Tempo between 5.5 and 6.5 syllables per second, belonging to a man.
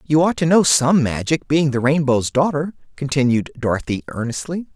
No: 5.1 syllables/s; male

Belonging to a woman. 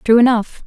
Yes: female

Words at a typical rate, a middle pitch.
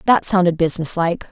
Yes: average, 180 wpm; medium, 180 Hz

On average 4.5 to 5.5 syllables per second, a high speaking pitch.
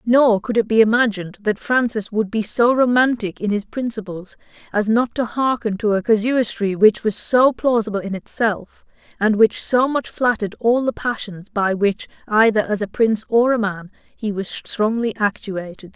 Yes: 4.8 syllables/s; high, 220 Hz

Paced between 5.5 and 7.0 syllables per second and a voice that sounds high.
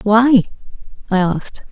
No: 4.4 syllables/s; high, 210 Hz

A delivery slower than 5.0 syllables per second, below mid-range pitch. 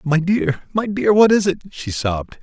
No: 4.5 syllables/s; medium, 175 Hz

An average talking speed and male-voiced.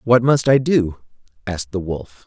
Yes: average, 185 wpm; male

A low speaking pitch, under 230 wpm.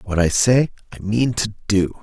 Yes: low, 110 Hz; fast, 205 wpm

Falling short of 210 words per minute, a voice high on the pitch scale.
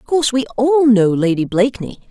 Yes: average, 200 wpm; high, 240 Hz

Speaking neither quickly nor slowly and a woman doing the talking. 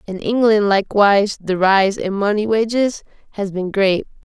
Yes: average, 150 wpm; female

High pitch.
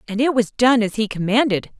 Yes: high, 225 Hz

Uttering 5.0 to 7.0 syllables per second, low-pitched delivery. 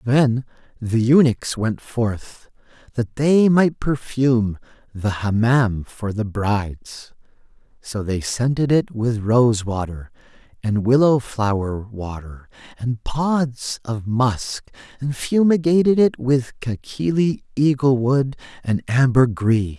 No: 3.6 syllables/s; low, 120 Hz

